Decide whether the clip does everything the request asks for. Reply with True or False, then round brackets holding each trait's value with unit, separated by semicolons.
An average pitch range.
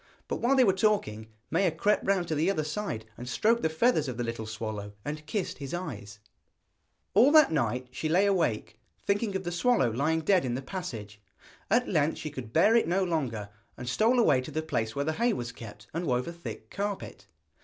False (8.3 semitones)